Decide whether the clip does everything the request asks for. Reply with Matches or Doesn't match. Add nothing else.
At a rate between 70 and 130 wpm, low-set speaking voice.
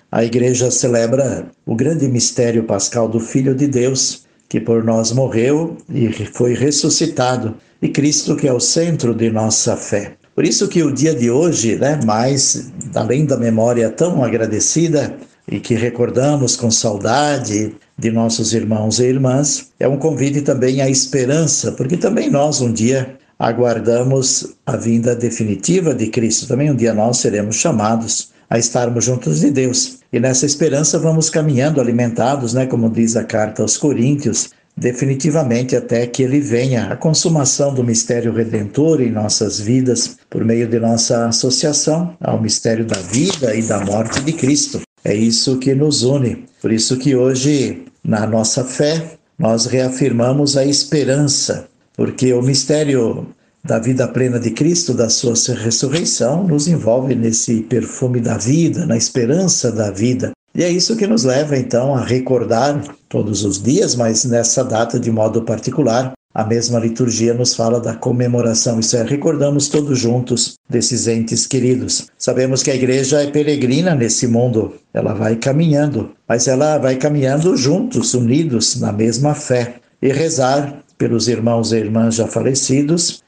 Doesn't match